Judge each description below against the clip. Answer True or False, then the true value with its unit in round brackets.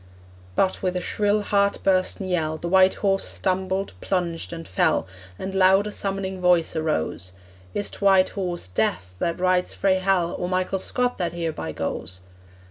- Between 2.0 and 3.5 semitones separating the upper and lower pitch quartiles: True (2.4 semitones)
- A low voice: False (185 Hz)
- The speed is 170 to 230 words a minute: False (160 wpm)